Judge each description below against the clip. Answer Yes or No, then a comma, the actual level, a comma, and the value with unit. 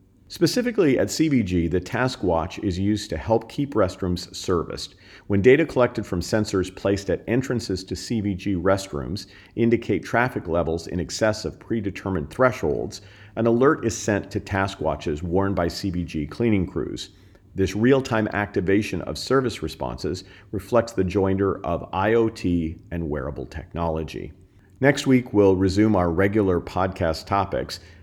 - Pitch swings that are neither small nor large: Yes, average, 3.7 semitones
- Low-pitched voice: Yes, low, 100 Hz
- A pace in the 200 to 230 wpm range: No, average, 145 wpm